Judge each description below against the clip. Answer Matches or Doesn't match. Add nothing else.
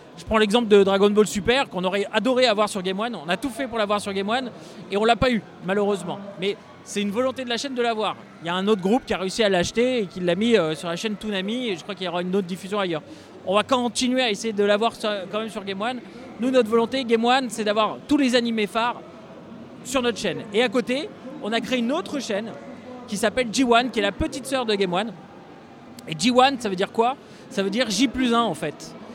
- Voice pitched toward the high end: Matches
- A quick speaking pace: Matches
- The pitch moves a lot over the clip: Doesn't match